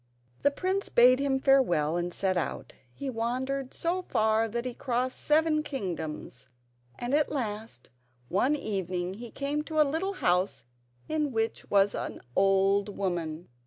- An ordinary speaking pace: Yes, average, 150 wpm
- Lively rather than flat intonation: Yes, wide, 6.6 semitones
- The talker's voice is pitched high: Yes, high, 235 Hz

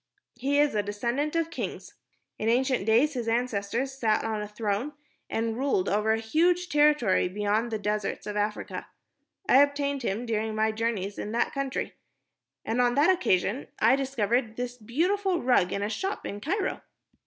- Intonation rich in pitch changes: No, average, 5.0 semitones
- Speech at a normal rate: Yes, average, 170 wpm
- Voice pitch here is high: Yes, high, 235 Hz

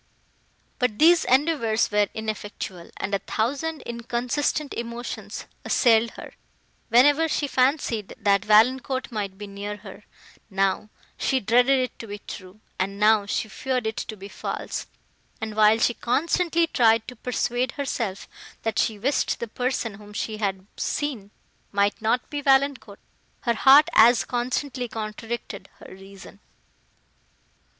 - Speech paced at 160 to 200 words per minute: No, average, 140 wpm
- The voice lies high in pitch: Yes, high, 230 Hz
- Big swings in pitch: No, average, 3.8 semitones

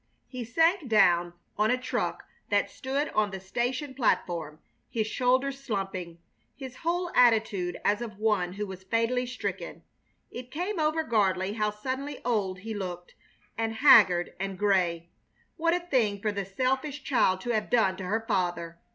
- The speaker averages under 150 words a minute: No, average, 160 wpm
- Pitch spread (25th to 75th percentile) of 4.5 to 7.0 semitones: Yes, wide, 5.4 semitones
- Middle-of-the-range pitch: No, high, 220 Hz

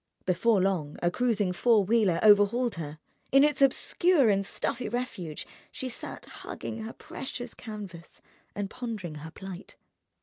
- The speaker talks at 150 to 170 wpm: No, average, 140 wpm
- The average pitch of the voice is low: No, high, 210 Hz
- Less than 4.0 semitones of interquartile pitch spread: No, average, 5.0 semitones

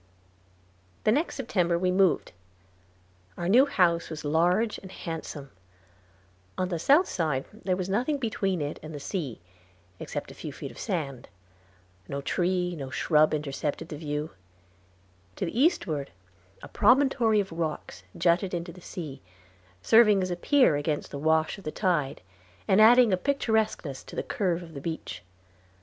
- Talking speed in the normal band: Yes, average, 160 wpm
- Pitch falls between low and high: Yes, medium, 175 Hz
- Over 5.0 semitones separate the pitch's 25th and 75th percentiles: Yes, wide, 5.4 semitones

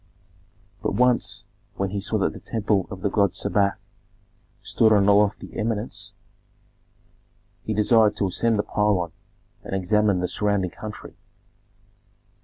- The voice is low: Yes, low, 105 Hz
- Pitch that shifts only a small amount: Yes, narrow, 1.6 semitones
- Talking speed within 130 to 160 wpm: Yes, slow, 135 wpm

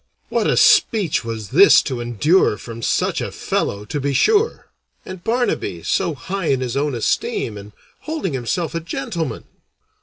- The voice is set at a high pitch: No, medium, 140 Hz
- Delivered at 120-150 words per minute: No, average, 160 wpm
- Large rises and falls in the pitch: Yes, wide, 8.1 semitones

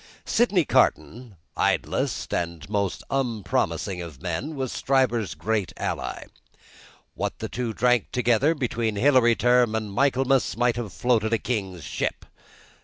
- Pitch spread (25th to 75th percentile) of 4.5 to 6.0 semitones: No, average, 3.8 semitones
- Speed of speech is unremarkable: No, slow, 130 wpm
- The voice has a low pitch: Yes, low, 120 Hz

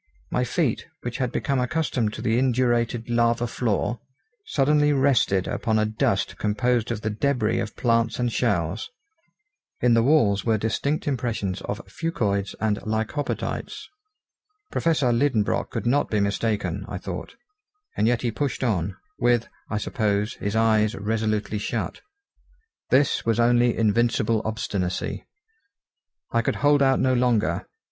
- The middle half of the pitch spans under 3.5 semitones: Yes, average, 2.8 semitones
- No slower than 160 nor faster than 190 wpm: No, average, 140 wpm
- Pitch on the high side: No, low, 115 Hz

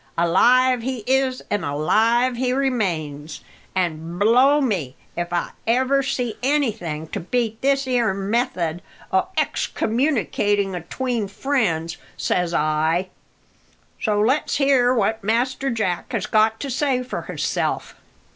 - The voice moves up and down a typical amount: No, wide, 6.4 semitones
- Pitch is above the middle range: Yes, high, 225 Hz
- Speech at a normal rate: No, slow, 125 wpm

